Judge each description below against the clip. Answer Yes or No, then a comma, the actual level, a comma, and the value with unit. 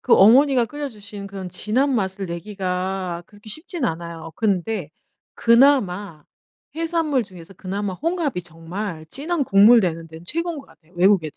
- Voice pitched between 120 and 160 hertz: No, high, 200 Hz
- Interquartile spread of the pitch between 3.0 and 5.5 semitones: No, wide, 6.6 semitones